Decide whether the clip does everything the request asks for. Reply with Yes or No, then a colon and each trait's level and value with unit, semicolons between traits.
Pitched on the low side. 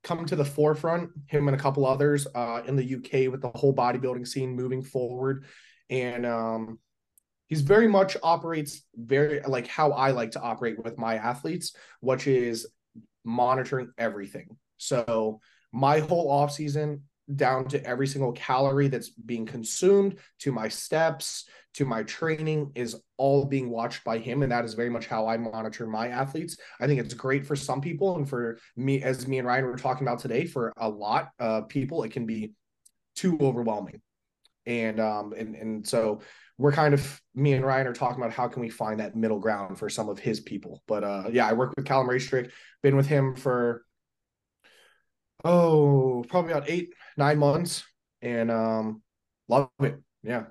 Yes: low, 130 Hz